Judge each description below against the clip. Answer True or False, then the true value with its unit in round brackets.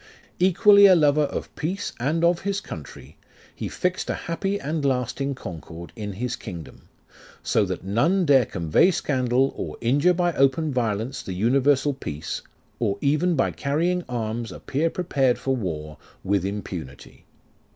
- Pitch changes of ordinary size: False (7.5 semitones)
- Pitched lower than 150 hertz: True (135 Hz)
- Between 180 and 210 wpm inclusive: False (150 wpm)